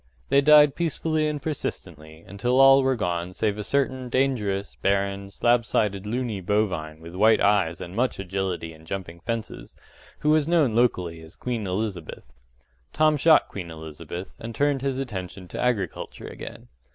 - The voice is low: Yes, low, 105 Hz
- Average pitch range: No, wide, 6.5 semitones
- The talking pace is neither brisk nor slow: Yes, average, 160 wpm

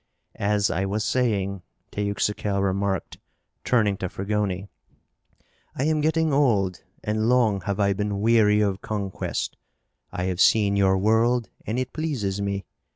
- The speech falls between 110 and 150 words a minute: Yes, average, 140 wpm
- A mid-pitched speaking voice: No, low, 105 Hz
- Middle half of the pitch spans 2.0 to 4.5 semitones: Yes, narrow, 2.6 semitones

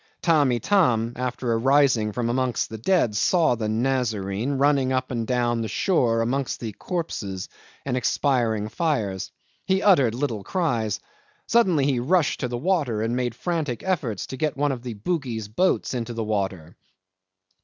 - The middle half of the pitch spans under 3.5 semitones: No, average, 4.4 semitones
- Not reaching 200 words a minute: Yes, average, 165 wpm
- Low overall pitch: Yes, low, 125 Hz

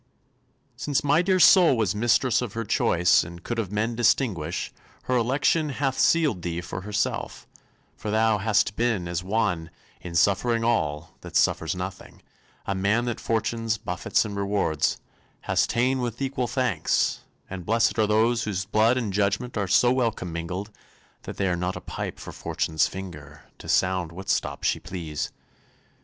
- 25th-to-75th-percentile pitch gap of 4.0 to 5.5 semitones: Yes, average, 4.7 semitones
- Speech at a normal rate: Yes, average, 165 wpm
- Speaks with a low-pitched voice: Yes, low, 105 Hz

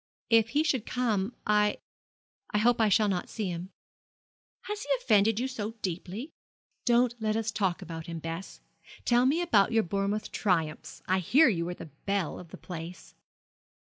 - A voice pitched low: No, high, 210 Hz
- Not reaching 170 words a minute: No, average, 175 wpm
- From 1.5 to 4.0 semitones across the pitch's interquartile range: No, average, 4.7 semitones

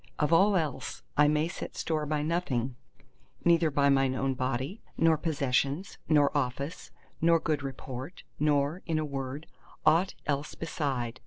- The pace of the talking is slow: No, average, 145 wpm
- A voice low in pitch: No, medium, 150 Hz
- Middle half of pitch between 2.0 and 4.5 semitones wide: Yes, average, 3.2 semitones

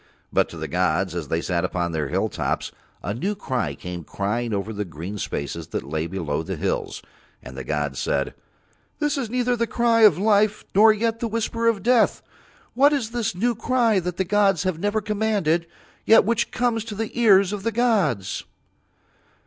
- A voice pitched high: Yes, high, 195 Hz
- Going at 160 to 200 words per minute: Yes, average, 190 wpm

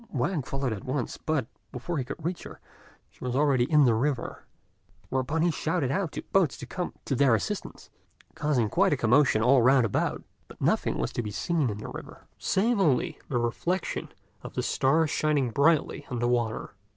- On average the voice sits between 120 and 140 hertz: Yes, low, 135 Hz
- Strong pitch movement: No, average, 4.4 semitones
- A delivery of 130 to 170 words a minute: No, average, 195 wpm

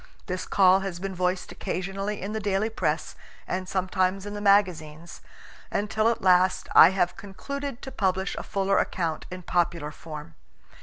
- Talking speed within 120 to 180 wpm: Yes, average, 160 wpm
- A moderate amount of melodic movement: No, narrow, 1.9 semitones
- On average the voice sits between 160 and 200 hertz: Yes, high, 190 Hz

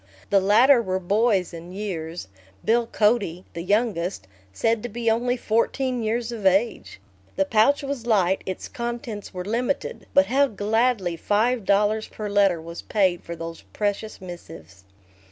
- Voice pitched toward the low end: No, high, 210 Hz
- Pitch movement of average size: Yes, average, 4.2 semitones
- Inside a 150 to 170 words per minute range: Yes, average, 155 wpm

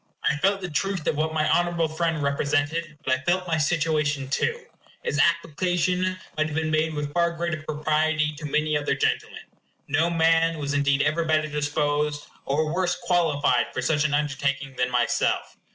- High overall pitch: No, medium, 155 Hz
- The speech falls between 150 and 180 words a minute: Yes, average, 175 wpm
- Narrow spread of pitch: Yes, narrow, 2.3 semitones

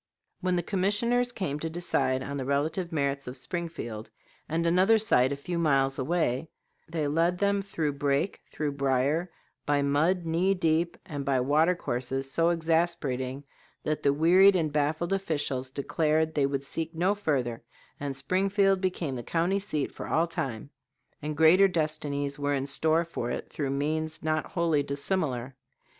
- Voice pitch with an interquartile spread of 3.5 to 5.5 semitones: Yes, average, 3.8 semitones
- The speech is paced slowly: No, average, 160 wpm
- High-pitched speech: No, medium, 155 Hz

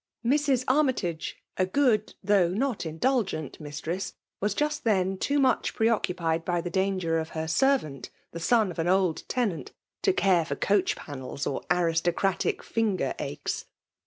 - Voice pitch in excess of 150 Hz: Yes, high, 190 Hz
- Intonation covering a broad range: Yes, wide, 6.1 semitones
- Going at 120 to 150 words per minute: No, average, 160 wpm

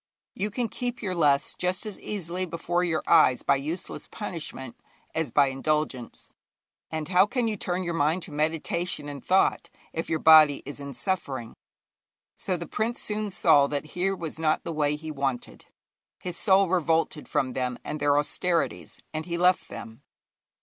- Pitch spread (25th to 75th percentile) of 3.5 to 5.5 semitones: Yes, average, 4.0 semitones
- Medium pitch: Yes, medium, 160 Hz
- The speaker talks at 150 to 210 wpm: Yes, average, 170 wpm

